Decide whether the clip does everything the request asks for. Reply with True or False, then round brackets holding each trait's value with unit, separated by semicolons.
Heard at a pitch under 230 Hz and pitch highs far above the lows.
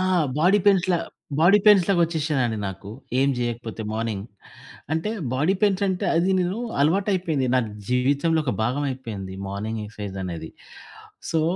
True (140 Hz; 8.0 semitones)